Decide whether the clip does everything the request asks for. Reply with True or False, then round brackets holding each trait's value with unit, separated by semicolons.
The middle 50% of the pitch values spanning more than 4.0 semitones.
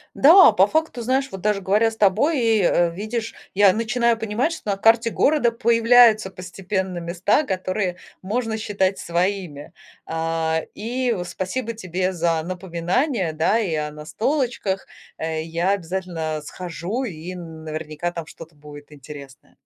True (5.2 semitones)